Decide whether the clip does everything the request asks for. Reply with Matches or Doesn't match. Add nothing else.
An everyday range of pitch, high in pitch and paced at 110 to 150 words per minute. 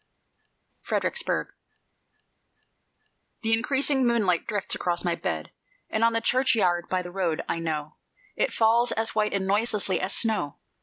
Matches